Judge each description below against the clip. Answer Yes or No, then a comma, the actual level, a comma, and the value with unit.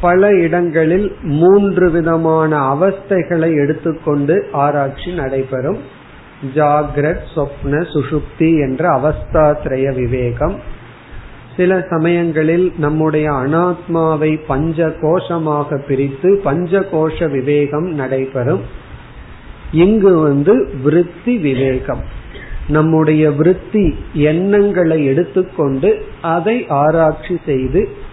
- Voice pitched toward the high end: No, medium, 155 Hz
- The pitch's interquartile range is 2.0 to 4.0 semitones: Yes, average, 3.5 semitones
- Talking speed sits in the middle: No, slow, 70 wpm